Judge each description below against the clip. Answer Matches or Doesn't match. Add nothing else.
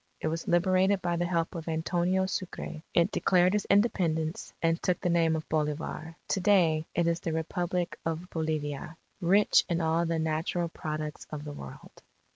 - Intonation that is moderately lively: Doesn't match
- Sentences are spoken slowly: Doesn't match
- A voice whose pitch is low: Doesn't match